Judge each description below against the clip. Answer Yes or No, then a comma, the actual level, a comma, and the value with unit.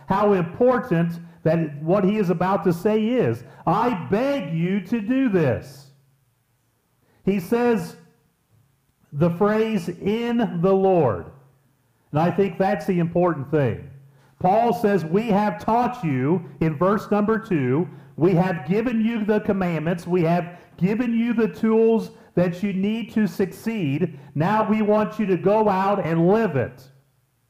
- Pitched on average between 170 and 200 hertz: Yes, medium, 185 Hz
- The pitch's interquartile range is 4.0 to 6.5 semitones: Yes, wide, 5.4 semitones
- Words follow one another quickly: No, average, 145 wpm